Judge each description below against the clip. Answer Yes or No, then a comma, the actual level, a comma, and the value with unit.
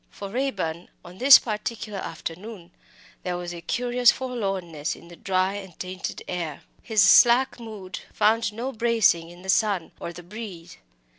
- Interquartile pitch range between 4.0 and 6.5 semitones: Yes, average, 4.6 semitones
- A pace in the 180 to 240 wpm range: No, average, 155 wpm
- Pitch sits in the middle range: No, high, 195 Hz